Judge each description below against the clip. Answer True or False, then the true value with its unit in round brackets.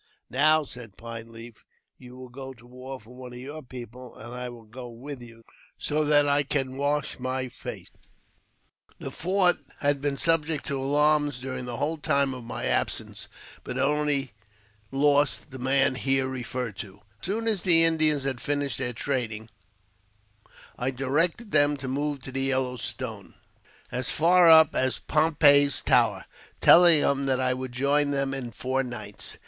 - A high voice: False (135 Hz)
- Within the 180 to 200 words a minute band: True (185 wpm)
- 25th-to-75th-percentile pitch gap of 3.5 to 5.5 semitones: False (2.8 semitones)